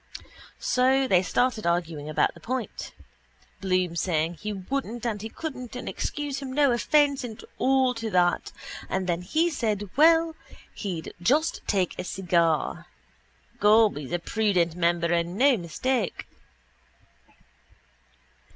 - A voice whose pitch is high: Yes, high, 210 Hz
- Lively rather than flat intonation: Yes, wide, 6.9 semitones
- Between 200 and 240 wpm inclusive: No, slow, 135 wpm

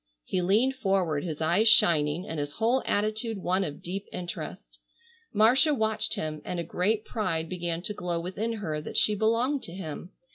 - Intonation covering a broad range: No, average, 4.6 semitones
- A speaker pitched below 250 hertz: Yes, high, 190 Hz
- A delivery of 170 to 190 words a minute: Yes, average, 180 wpm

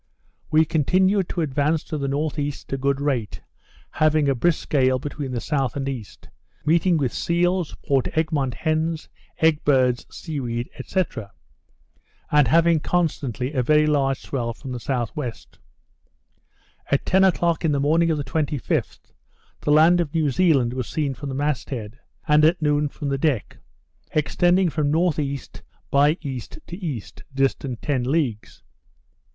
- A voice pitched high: No, medium, 145 Hz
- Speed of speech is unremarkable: Yes, average, 155 wpm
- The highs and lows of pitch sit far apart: No, average, 3.1 semitones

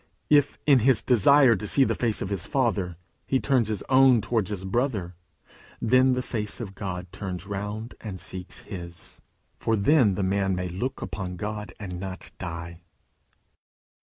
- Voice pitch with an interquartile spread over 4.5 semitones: Yes, average, 4.9 semitones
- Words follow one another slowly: No, average, 165 wpm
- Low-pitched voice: Yes, low, 105 Hz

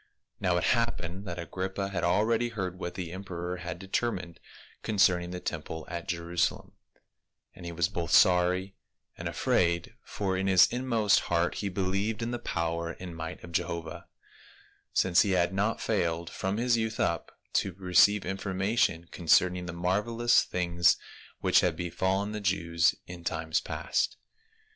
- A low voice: Yes, very low, 90 Hz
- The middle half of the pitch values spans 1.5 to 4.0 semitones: Yes, narrow, 2.5 semitones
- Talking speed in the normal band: Yes, average, 155 wpm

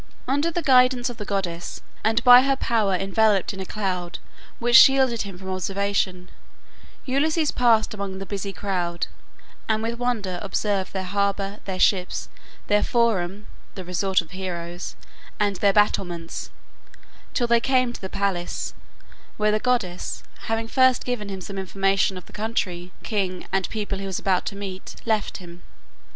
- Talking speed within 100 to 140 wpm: No, average, 160 wpm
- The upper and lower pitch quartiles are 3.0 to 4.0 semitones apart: Yes, average, 3.5 semitones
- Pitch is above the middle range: Yes, high, 200 Hz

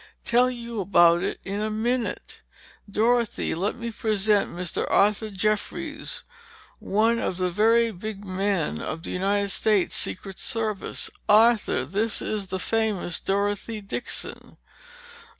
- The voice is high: Yes, high, 210 Hz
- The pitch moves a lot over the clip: No, average, 2.7 semitones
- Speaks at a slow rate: Yes, slow, 130 wpm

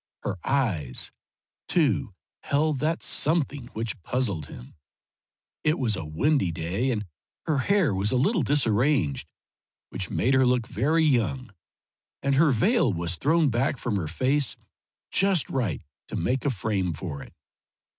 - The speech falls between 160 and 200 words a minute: No, average, 145 wpm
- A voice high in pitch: No, low, 125 Hz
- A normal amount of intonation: No, wide, 7.3 semitones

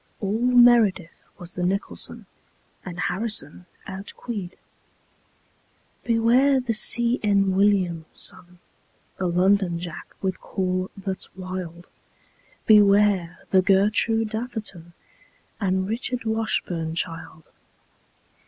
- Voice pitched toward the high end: Yes, high, 195 Hz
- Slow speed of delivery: Yes, slow, 85 wpm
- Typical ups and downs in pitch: Yes, average, 3.6 semitones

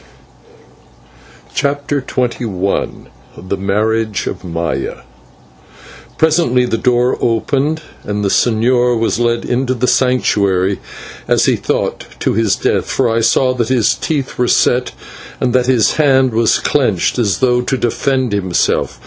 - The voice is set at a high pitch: No, low, 120 Hz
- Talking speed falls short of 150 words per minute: Yes, slow, 135 wpm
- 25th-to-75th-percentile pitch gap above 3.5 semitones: No, average, 3.2 semitones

